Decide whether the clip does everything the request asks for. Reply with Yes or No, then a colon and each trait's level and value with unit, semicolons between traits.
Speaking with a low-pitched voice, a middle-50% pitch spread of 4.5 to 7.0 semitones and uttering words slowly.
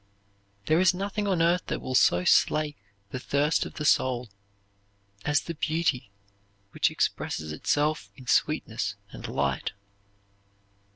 No: medium, 150 Hz; average, 5.1 semitones; slow, 130 wpm